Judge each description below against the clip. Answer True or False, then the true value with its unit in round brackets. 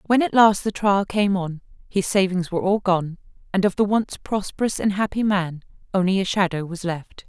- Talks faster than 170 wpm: True (205 wpm)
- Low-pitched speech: False (190 Hz)